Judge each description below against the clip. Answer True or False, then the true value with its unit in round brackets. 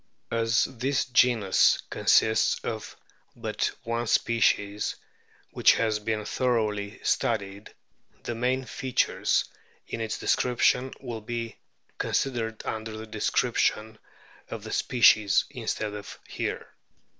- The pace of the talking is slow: True (110 wpm)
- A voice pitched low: True (115 Hz)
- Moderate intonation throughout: False (2.1 semitones)